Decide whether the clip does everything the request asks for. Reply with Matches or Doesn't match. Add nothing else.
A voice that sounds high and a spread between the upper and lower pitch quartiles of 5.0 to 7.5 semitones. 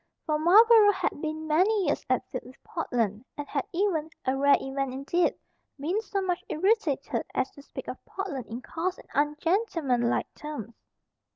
Matches